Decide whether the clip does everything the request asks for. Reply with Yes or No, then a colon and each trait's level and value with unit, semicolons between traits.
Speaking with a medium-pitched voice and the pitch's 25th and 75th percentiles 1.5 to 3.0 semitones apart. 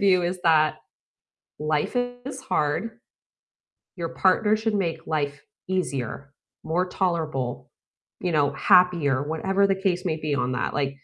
No: medium, 165 Hz; average, 4.3 semitones